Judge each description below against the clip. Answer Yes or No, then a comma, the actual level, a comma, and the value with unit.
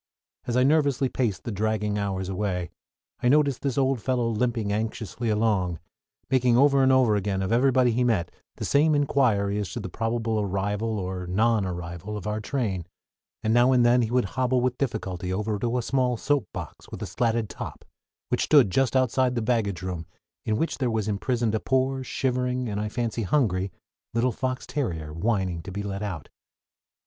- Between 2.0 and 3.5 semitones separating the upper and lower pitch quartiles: No, average, 4.1 semitones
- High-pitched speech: No, low, 115 Hz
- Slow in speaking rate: No, average, 190 wpm